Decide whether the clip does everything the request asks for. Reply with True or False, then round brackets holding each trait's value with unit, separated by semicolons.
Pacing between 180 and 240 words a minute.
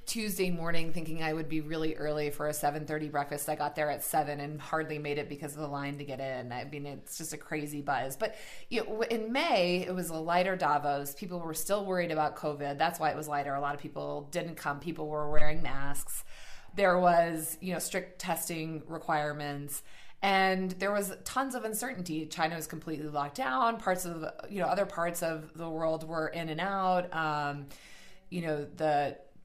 True (205 wpm)